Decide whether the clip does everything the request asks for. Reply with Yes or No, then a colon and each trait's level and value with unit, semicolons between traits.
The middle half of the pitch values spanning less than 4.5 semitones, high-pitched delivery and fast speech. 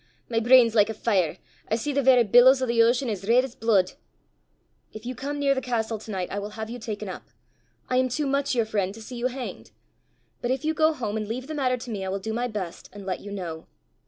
Yes: average, 3.6 semitones; high, 230 Hz; fast, 265 wpm